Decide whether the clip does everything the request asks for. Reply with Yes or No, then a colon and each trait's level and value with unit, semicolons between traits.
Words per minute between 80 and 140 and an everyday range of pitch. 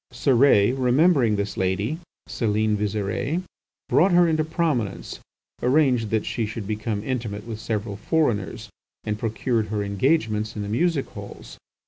Yes: slow, 135 wpm; average, 4.5 semitones